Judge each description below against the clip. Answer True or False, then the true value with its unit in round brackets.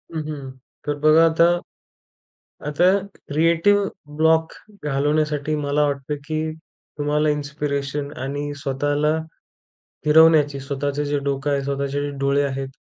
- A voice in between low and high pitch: True (145 Hz)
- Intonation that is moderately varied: False (1.5 semitones)